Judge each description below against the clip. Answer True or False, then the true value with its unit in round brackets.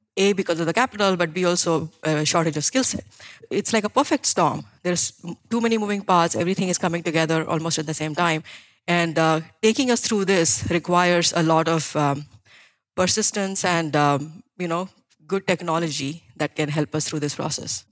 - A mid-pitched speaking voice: True (170 Hz)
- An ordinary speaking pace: True (190 wpm)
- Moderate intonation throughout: True (3.4 semitones)